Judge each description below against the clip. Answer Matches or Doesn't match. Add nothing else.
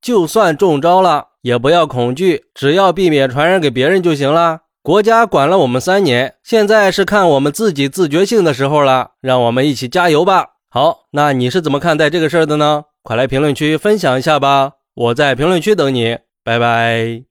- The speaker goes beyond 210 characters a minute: Matches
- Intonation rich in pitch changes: Matches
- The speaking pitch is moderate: Matches